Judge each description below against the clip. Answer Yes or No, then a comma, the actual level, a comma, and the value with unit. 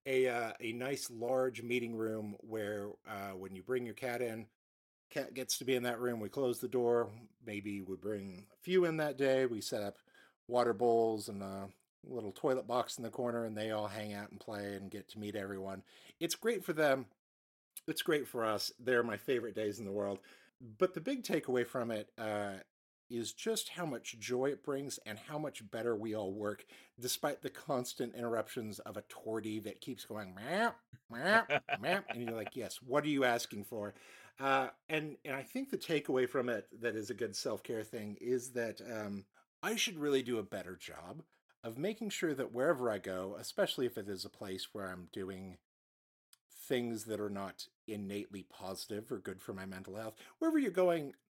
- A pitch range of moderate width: Yes, average, 4.1 semitones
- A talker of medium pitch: No, low, 115 Hz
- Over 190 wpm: Yes, average, 200 wpm